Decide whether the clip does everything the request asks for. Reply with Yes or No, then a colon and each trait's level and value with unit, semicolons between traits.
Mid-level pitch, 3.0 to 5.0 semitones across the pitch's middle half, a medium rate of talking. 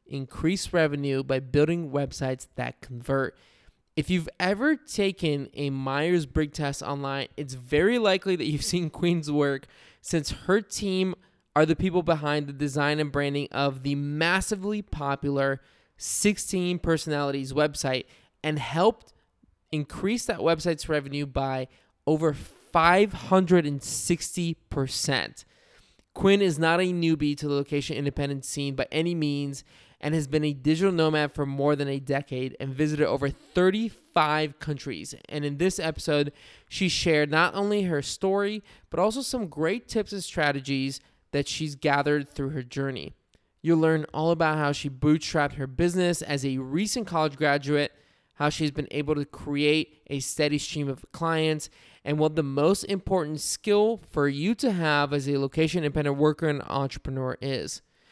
Yes: medium, 150 Hz; average, 3.3 semitones; average, 150 wpm